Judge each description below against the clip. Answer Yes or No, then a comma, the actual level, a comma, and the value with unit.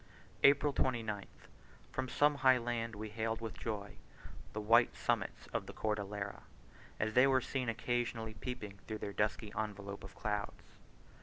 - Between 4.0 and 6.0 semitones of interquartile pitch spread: No, average, 2.7 semitones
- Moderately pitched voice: No, low, 110 Hz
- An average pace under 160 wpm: Yes, average, 150 wpm